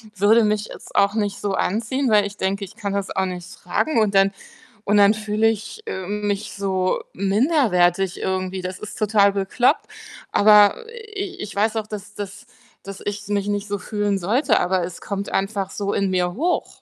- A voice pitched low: No, high, 205 Hz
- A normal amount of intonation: No, narrow, 1.8 semitones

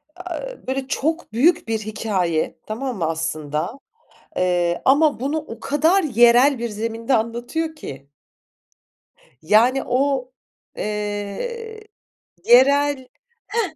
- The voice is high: Yes, high, 245 Hz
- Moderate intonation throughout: No, wide, 5.7 semitones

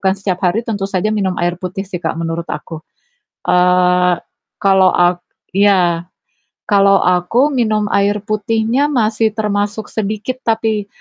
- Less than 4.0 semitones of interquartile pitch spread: Yes, average, 3.1 semitones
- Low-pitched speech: No, high, 200 Hz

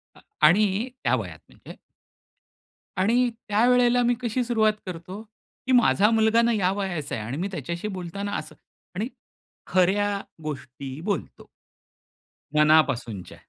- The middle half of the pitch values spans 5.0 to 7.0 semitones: Yes, wide, 5.5 semitones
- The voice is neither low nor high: No, high, 195 Hz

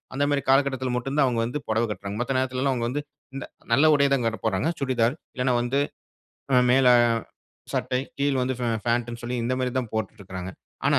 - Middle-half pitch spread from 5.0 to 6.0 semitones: No, narrow, 2.5 semitones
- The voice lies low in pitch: Yes, low, 125 Hz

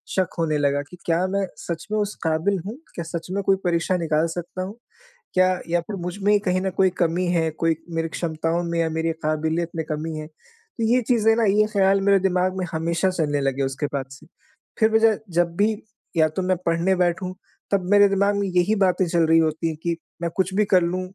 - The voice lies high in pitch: No, medium, 175 Hz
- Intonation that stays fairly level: No, average, 3.1 semitones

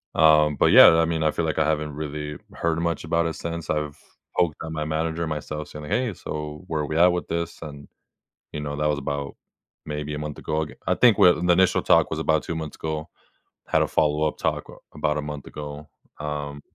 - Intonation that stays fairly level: Yes, narrow, 1.6 semitones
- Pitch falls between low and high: No, very low, 75 Hz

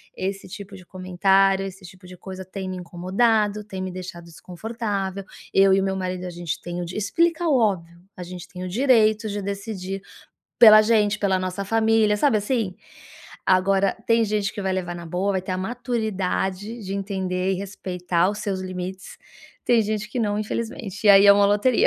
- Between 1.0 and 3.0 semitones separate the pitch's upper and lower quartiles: Yes, narrow, 2.5 semitones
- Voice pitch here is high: Yes, high, 195 Hz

